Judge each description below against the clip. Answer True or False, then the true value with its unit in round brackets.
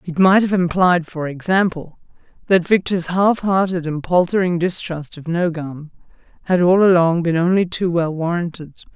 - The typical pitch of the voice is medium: True (175 Hz)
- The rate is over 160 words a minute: False (155 wpm)